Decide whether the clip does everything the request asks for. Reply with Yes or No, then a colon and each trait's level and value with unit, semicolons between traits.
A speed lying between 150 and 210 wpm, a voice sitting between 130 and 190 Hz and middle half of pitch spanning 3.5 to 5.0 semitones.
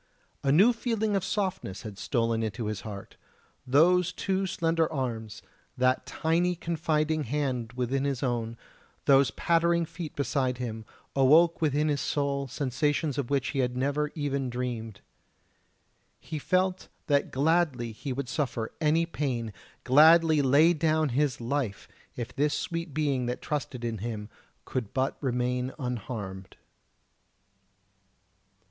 No: slow, 135 wpm; medium, 140 Hz; average, 4.5 semitones